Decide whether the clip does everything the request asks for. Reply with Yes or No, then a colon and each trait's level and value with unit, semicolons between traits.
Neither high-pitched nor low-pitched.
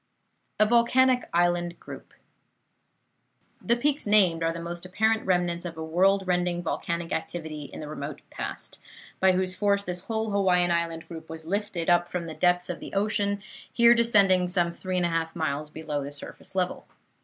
Yes: medium, 180 Hz